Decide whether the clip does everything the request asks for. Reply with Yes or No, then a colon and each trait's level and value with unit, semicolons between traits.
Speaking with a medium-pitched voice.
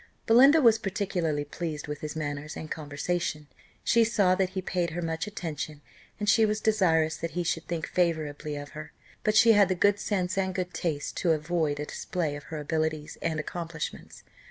Yes: medium, 170 Hz